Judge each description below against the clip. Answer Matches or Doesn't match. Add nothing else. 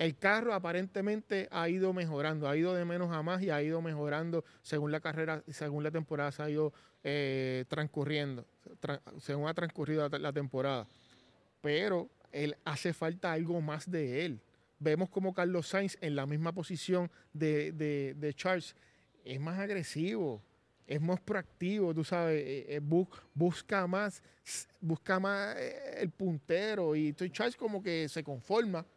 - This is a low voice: Doesn't match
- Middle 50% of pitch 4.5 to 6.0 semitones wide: Doesn't match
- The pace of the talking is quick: Doesn't match